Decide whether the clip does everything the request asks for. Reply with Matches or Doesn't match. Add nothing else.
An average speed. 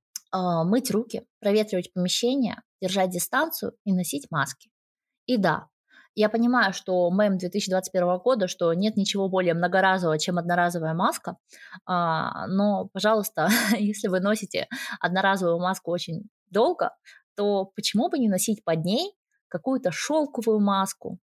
Matches